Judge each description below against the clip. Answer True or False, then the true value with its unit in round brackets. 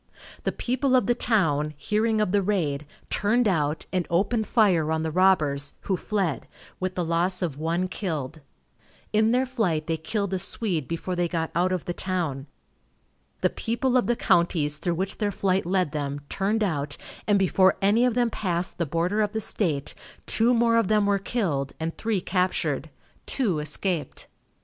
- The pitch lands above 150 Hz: True (185 Hz)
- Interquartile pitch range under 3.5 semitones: False (4.8 semitones)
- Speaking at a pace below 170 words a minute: False (180 wpm)